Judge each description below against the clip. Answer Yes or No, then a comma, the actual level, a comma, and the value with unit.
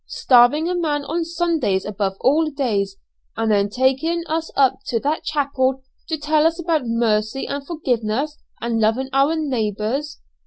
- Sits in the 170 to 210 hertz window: No, very high, 275 Hz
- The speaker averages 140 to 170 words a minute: Yes, average, 155 wpm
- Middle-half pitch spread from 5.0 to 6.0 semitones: Yes, wide, 5.5 semitones